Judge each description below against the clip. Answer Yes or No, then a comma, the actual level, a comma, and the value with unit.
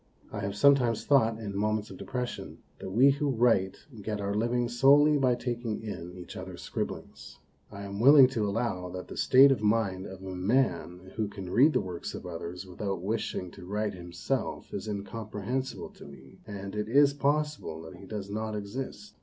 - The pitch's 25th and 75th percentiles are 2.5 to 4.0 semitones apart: No, average, 4.5 semitones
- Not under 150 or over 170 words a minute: No, average, 185 wpm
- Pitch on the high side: No, low, 105 Hz